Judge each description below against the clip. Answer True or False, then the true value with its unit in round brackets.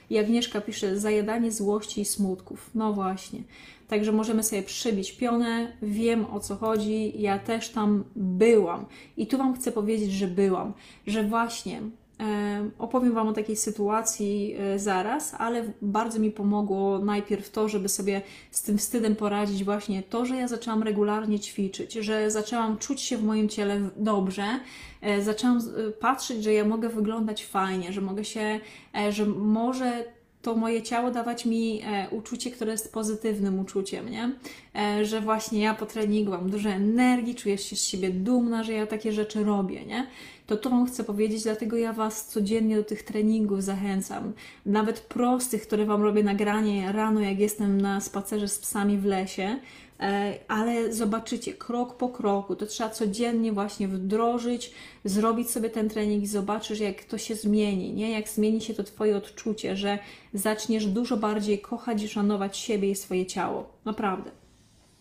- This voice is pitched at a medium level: False (215 Hz)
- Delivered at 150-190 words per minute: True (160 wpm)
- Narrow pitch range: True (1.8 semitones)